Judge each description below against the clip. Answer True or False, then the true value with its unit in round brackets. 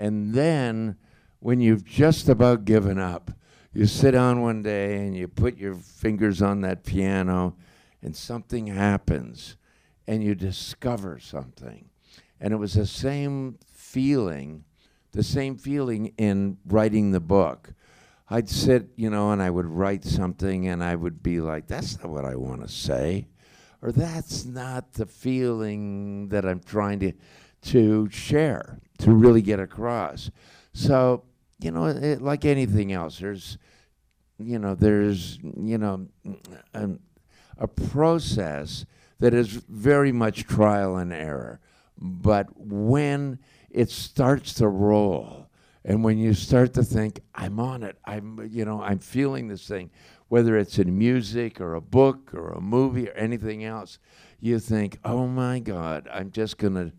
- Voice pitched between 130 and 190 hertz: False (105 Hz)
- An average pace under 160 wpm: True (150 wpm)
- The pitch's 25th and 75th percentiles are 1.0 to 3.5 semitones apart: False (4.1 semitones)